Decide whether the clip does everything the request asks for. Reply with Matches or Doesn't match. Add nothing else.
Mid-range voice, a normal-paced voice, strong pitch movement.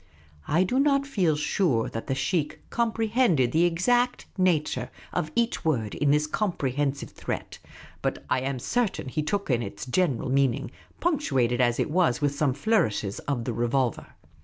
Matches